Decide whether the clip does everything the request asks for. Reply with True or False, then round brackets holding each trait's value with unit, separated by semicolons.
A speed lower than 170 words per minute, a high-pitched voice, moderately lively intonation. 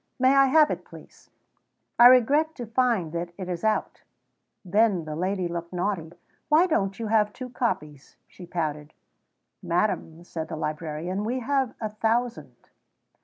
False (155 wpm; 200 Hz; 6.2 semitones)